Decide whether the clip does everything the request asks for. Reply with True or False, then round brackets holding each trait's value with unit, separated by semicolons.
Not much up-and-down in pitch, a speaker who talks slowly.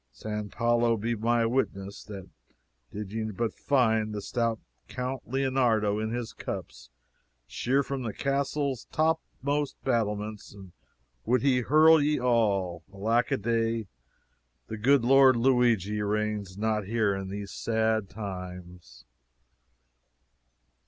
False (3.5 semitones; 120 wpm)